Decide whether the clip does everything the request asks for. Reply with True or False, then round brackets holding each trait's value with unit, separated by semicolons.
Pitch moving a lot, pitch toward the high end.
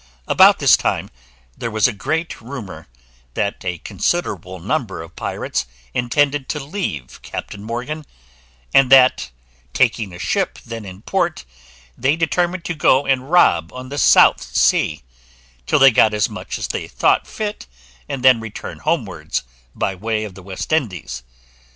False (7.0 semitones; 120 Hz)